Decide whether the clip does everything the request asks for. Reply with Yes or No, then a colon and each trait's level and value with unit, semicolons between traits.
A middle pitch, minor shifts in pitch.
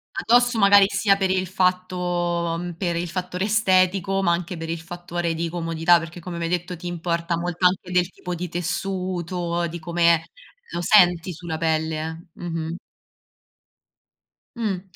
Yes: medium, 175 Hz; narrow, 1.7 semitones